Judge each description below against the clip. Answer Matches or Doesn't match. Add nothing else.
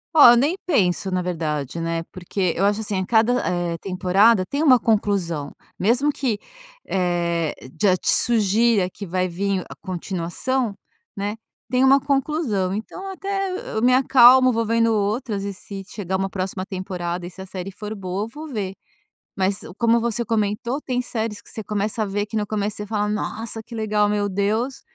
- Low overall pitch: Doesn't match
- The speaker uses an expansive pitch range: Doesn't match